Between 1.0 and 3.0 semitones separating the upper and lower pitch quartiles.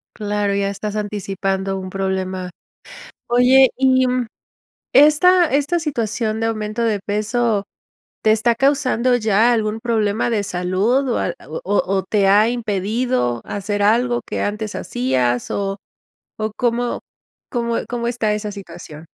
No: average, 3.5 semitones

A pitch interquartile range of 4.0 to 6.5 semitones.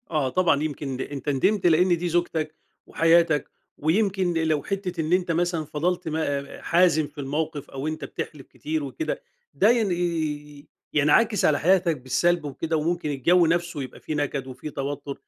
No: average, 3.3 semitones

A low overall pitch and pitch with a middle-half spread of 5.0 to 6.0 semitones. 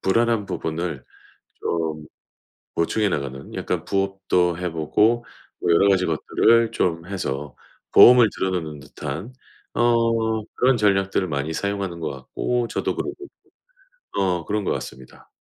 Yes: very low, 95 Hz; wide, 5.4 semitones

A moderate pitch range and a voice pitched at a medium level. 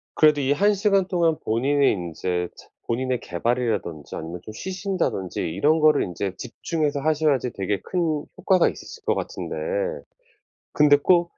No: wide, 8.4 semitones; medium, 145 Hz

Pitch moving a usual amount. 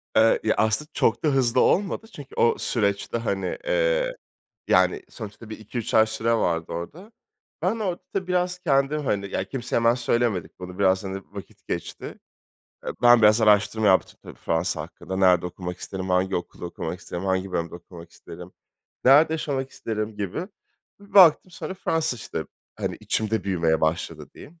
No: wide, 7.8 semitones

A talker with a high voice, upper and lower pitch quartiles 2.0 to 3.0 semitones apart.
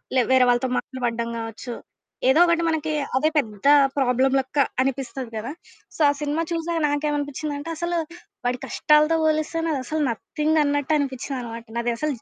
No: very high, 285 Hz; average, 3.6 semitones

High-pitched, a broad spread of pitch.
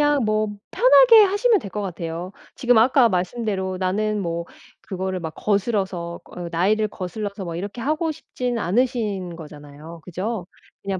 No: high, 200 Hz; average, 4.7 semitones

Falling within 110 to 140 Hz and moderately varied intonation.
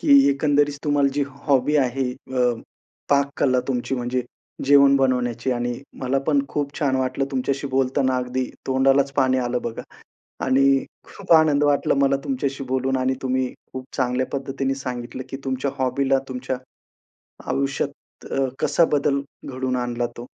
No: low, 135 Hz; narrow, 1.6 semitones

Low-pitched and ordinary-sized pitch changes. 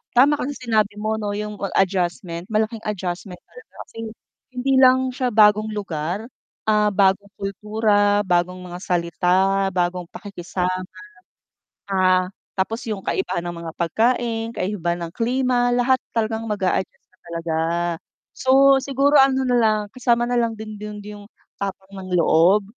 No: high, 210 Hz; average, 3.9 semitones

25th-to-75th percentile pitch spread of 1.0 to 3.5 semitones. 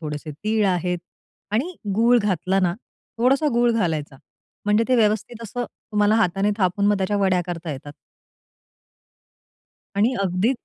No: average, 4.2 semitones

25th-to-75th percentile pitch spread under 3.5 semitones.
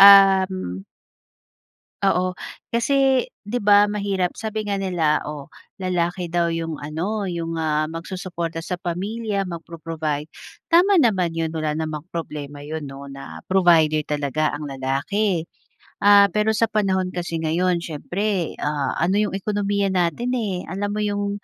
No: average, 4.2 semitones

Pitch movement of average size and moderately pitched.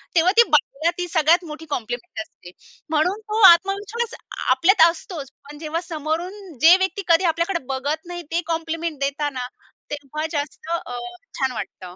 No: average, 3.5 semitones; very high, 325 Hz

